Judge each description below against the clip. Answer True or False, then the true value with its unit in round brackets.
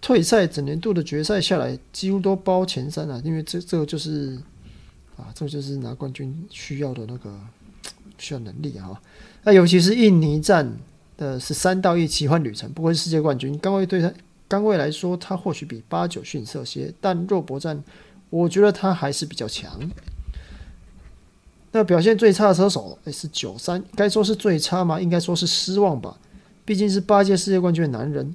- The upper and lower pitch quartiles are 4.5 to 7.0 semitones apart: True (5.5 semitones)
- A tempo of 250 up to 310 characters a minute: True (280 characters per minute)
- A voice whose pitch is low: False (165 Hz)